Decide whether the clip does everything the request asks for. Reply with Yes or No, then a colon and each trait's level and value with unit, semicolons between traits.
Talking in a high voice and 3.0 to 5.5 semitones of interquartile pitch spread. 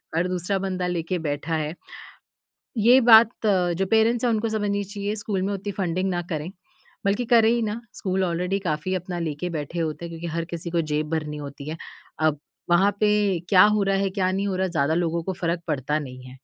No: medium, 180 Hz; average, 3.6 semitones